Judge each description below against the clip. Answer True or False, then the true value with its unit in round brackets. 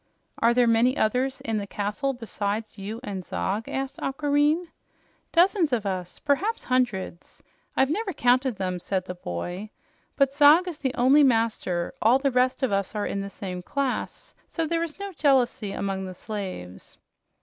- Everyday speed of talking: True (170 wpm)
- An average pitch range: False (5.9 semitones)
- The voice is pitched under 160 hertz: False (240 Hz)